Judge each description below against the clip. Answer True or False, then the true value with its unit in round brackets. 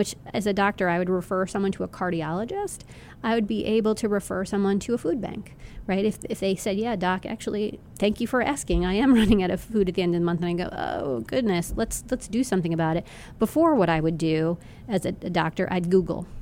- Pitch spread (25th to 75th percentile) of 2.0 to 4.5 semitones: True (3.6 semitones)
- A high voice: True (195 Hz)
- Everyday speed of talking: False (250 wpm)